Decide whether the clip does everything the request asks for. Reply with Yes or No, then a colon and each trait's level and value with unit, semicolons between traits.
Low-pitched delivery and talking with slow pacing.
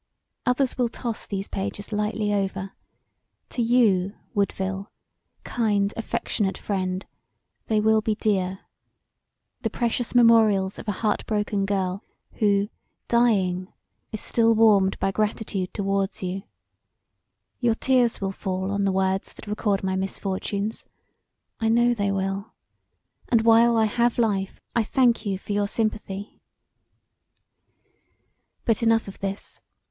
No: high, 205 Hz; slow, 130 wpm